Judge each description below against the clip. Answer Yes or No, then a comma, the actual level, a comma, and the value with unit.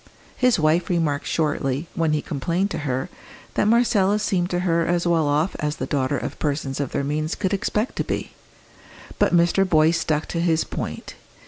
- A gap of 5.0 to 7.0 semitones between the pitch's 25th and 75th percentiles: No, average, 3.3 semitones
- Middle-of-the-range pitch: Yes, medium, 165 Hz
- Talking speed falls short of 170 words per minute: No, average, 190 wpm